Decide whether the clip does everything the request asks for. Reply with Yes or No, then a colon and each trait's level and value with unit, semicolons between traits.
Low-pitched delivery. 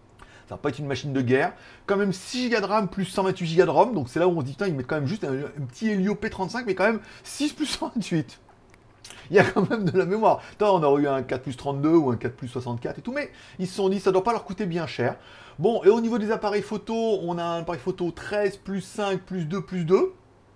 No: medium, 185 Hz